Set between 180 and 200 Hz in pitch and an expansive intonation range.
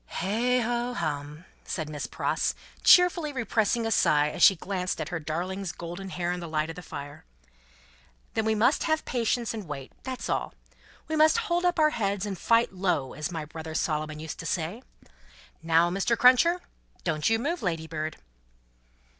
Yes: high, 190 Hz; wide, 6.9 semitones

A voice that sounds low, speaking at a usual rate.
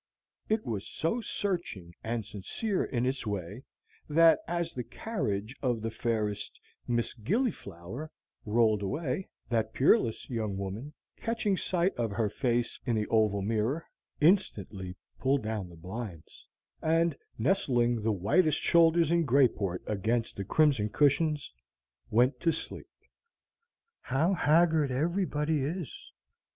No: low, 125 Hz; slow, 125 wpm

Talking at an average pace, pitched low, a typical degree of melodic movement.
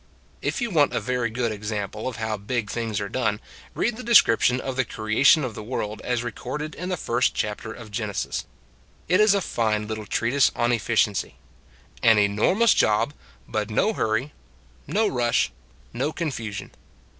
Yes: average, 175 wpm; low, 115 Hz; average, 4.3 semitones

